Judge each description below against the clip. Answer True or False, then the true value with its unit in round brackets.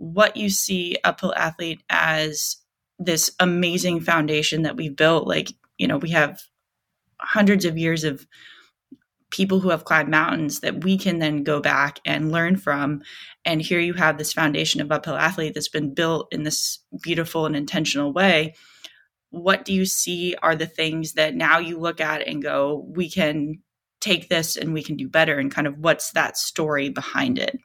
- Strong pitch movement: False (2.6 semitones)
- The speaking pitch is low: False (160 Hz)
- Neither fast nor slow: True (180 wpm)